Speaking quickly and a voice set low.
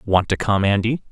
Yes: fast, 215 wpm; low, 105 Hz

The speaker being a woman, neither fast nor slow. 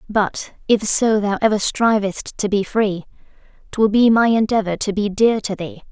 Yes: female; average, 185 wpm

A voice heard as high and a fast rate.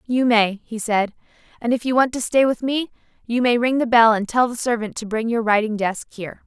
Yes: high, 230 Hz; fast, 250 wpm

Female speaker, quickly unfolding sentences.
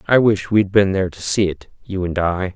No: male; fast, 280 wpm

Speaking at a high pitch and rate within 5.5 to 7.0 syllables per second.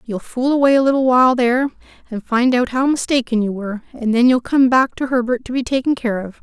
Yes: very high, 250 Hz; 6.0 syllables/s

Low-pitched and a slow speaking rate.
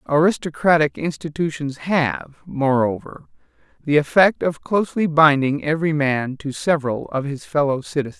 No: medium, 150 Hz; slow, 125 wpm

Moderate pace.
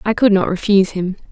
No: fast, 230 wpm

